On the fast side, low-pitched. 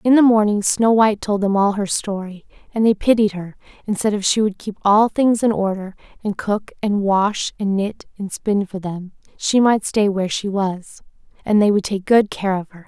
No: fast, 225 wpm; high, 205 Hz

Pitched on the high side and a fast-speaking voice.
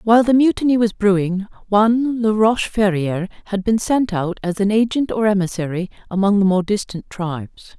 No: high, 205 Hz; average, 175 wpm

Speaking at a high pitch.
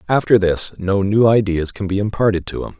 No: low, 100 Hz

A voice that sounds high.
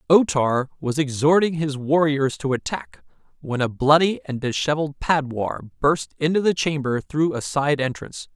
No: medium, 145 Hz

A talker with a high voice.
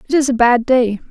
Yes: very high, 250 Hz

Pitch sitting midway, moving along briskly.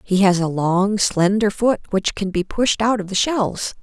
No: high, 200 Hz; fast, 220 wpm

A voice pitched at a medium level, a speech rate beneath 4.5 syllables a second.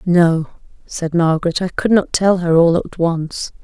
Yes: medium, 170 Hz; 4.2 syllables/s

